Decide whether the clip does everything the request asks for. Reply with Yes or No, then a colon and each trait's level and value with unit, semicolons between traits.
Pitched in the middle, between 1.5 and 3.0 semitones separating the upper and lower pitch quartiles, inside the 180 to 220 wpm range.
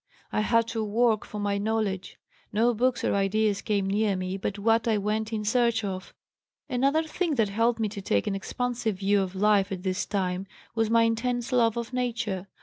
No: high, 215 Hz; average, 2.7 semitones; average, 200 wpm